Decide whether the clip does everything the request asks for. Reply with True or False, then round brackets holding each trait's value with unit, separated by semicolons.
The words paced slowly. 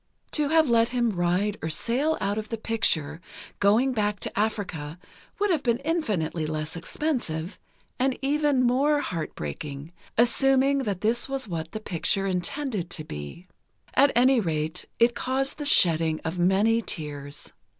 False (150 wpm)